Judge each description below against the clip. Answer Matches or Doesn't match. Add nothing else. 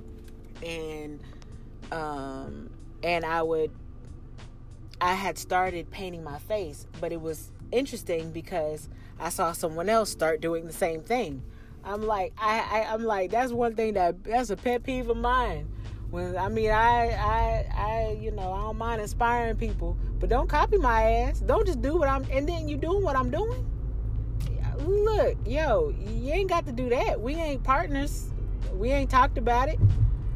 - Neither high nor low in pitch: Matches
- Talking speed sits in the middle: Matches